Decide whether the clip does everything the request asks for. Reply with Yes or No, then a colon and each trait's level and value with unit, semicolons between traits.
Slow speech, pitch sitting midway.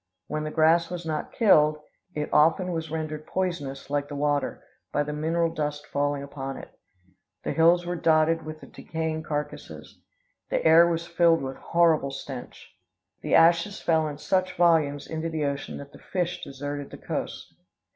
No: average, 170 wpm; medium, 155 Hz